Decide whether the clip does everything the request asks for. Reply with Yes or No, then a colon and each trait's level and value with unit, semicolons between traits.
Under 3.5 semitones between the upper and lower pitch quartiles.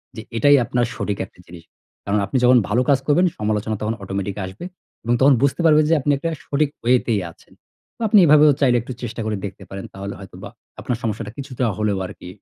No: wide, 5.6 semitones